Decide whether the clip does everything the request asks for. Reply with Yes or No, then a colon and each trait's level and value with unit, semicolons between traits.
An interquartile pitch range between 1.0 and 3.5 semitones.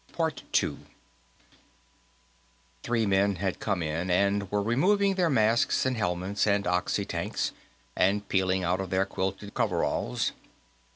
Yes: average, 2.9 semitones